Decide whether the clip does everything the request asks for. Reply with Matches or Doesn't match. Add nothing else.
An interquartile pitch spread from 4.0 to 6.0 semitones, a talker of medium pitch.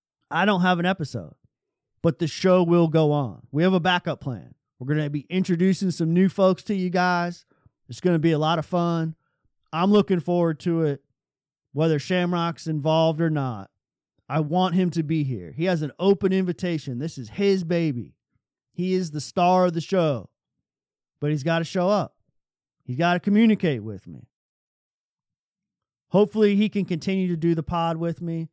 Doesn't match